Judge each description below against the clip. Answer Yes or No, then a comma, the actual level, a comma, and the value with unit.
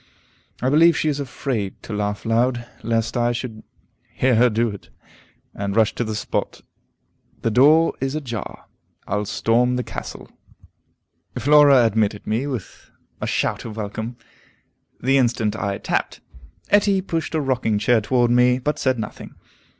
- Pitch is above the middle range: No, low, 120 Hz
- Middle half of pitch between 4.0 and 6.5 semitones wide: No, average, 3.5 semitones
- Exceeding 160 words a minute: No, average, 150 wpm